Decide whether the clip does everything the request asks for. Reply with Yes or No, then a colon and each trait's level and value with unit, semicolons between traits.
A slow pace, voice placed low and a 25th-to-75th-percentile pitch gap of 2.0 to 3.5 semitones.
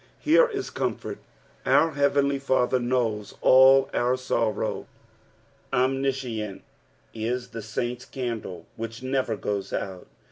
Yes: slow, 110 wpm; low, 125 Hz; average, 3.0 semitones